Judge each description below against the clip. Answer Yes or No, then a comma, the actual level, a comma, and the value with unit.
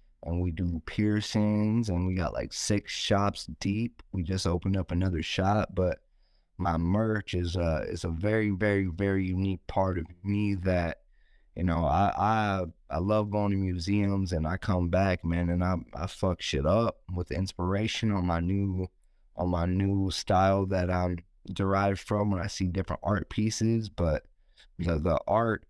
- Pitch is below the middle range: Yes, very low, 95 Hz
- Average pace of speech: Yes, average, 175 wpm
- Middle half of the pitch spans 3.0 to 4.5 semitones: No, narrow, 2.5 semitones